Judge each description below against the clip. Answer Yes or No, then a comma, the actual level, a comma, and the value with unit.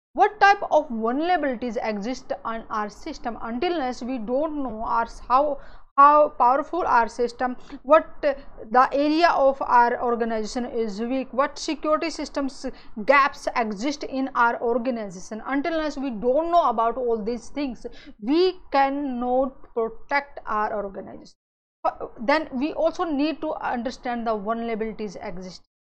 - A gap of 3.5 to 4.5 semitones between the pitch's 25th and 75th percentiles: Yes, average, 4.0 semitones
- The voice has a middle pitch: No, very high, 255 Hz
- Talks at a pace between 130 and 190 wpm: Yes, slow, 135 wpm